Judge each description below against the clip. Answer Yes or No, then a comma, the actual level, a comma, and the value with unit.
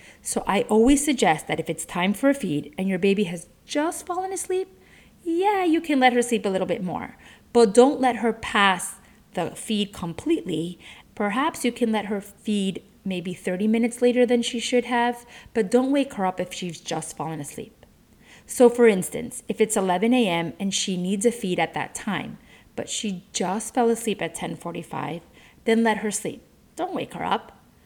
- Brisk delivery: No, average, 195 wpm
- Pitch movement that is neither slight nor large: Yes, average, 5.0 semitones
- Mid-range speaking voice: No, high, 215 Hz